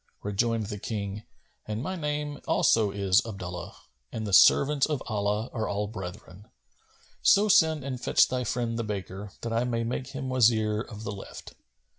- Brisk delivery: No, average, 175 wpm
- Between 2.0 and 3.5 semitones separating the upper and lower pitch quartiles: No, average, 4.0 semitones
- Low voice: Yes, low, 110 Hz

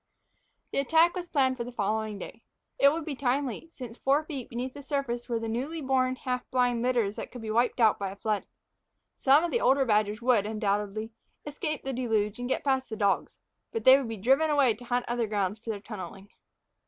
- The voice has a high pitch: Yes, high, 245 Hz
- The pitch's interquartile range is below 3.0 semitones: No, average, 3.9 semitones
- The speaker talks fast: Yes, fast, 215 wpm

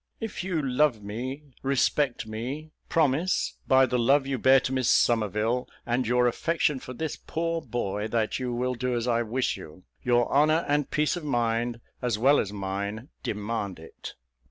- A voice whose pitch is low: Yes, low, 125 Hz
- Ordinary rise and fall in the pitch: Yes, average, 3.8 semitones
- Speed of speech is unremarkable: Yes, average, 175 wpm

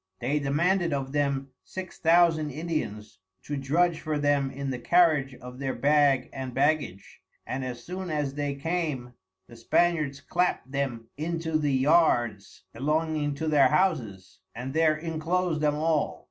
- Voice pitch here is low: No, medium, 145 Hz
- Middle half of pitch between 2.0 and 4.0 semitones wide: Yes, average, 3.3 semitones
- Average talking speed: Yes, average, 150 wpm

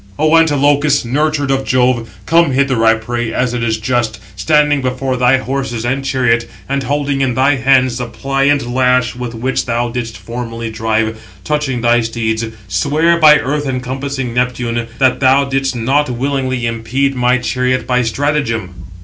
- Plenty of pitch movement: No, average, 2.7 semitones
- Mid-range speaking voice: No, low, 125 Hz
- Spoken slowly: No, average, 160 wpm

